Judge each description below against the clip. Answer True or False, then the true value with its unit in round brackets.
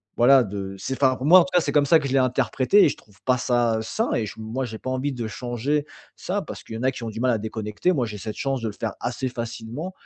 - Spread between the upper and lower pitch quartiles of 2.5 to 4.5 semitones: True (3.4 semitones)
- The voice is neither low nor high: False (125 Hz)